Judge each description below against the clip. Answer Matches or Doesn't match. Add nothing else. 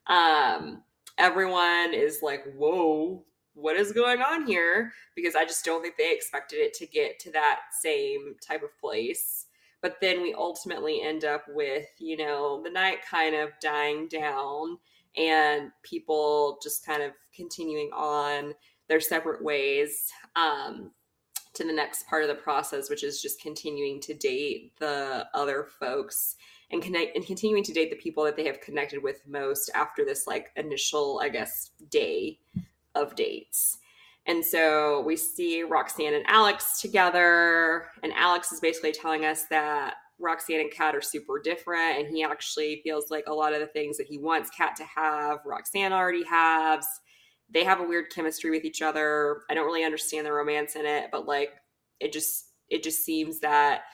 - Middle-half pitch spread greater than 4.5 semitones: Matches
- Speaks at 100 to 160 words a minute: Doesn't match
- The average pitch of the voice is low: Doesn't match